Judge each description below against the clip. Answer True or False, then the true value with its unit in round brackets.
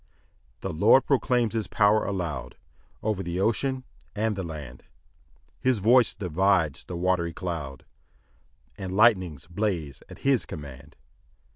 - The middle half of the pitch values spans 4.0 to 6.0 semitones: True (5.1 semitones)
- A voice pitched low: True (95 Hz)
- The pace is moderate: False (130 wpm)